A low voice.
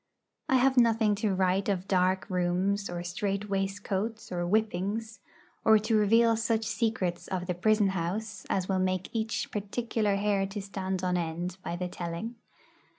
No: high, 195 Hz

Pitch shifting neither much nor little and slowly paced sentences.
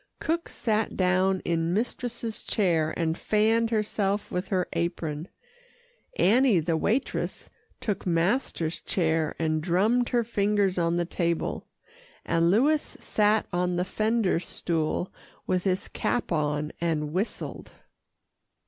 Yes: average, 4.5 semitones; slow, 120 wpm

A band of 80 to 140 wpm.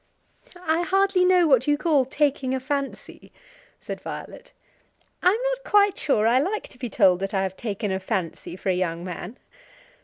No: average, 185 wpm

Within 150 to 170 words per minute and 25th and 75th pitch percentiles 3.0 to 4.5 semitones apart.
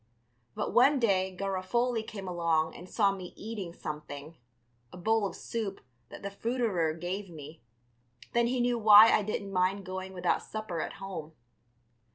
Yes: average, 160 wpm; average, 3.8 semitones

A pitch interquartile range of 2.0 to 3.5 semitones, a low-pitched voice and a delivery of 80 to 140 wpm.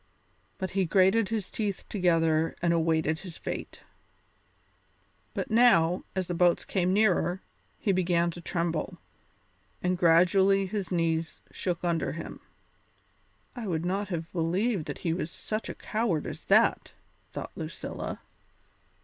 No: average, 2.7 semitones; medium, 180 Hz; slow, 135 wpm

